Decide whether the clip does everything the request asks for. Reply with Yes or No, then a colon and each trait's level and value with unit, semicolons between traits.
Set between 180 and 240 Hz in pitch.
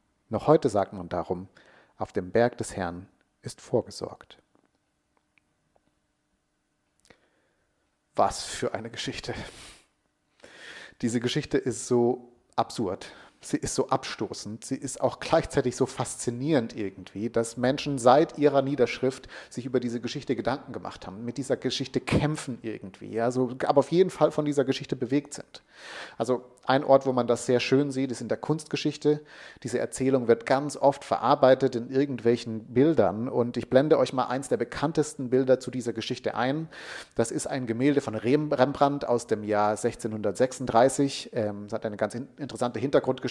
No: low, 130 Hz